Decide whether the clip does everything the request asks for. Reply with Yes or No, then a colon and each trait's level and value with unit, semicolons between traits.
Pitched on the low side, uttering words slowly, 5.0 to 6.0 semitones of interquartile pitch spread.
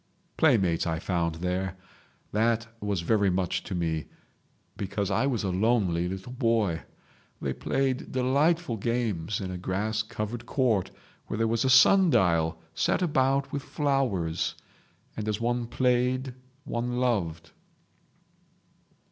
Yes: low, 110 Hz; slow, 130 wpm; wide, 5.5 semitones